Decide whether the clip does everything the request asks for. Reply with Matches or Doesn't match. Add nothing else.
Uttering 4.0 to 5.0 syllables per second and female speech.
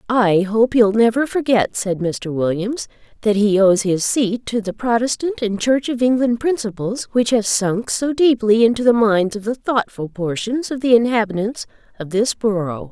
Matches